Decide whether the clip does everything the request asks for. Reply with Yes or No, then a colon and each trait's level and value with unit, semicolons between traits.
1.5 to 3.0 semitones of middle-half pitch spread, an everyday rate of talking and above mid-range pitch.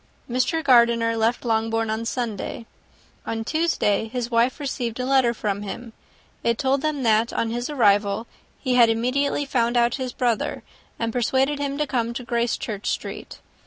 Yes: narrow, 2.5 semitones; average, 165 wpm; high, 235 Hz